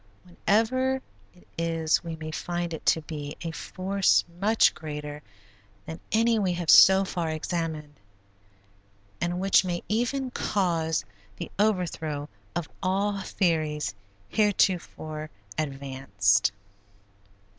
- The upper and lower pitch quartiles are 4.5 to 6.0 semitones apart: No, average, 4.0 semitones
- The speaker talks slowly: Yes, slow, 110 wpm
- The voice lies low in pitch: No, medium, 170 Hz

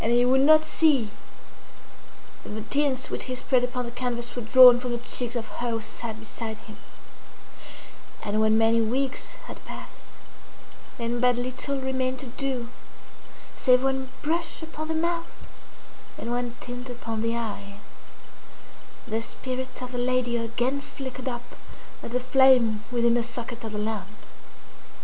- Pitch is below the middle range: No, high, 245 Hz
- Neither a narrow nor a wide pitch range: No, narrow, 2.2 semitones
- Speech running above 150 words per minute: Yes, average, 160 wpm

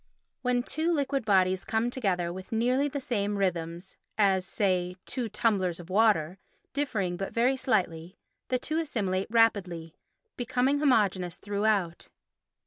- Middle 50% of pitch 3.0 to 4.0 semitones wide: No, average, 5.3 semitones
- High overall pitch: Yes, high, 205 Hz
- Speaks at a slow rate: Yes, slow, 130 wpm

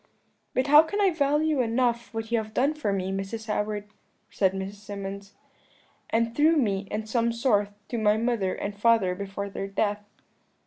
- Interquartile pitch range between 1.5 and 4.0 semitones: Yes, average, 3.2 semitones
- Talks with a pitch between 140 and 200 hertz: No, high, 215 Hz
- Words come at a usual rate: Yes, average, 175 wpm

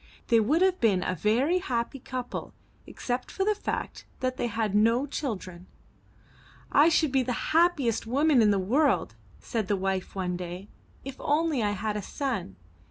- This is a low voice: No, high, 235 Hz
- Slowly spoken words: No, average, 170 wpm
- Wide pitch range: Yes, wide, 5.7 semitones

